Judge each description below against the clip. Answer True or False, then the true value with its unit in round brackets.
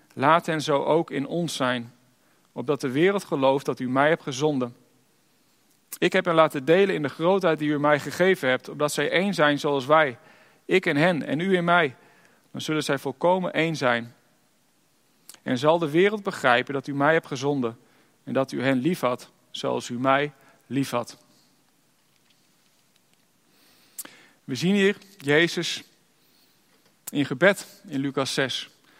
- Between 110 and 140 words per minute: False (160 wpm)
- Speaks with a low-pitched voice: False (145 Hz)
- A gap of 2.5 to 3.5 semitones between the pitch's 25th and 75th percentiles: False (4.0 semitones)